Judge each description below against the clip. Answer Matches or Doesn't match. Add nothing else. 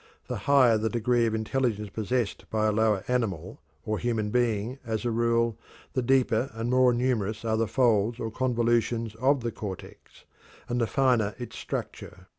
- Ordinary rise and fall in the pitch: Doesn't match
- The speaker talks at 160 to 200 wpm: Matches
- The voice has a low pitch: Matches